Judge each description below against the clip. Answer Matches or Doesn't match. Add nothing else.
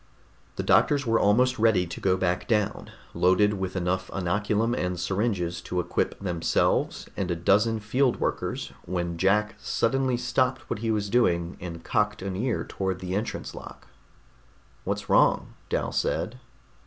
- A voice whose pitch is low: Matches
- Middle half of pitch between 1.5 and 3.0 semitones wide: Doesn't match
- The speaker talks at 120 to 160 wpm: Matches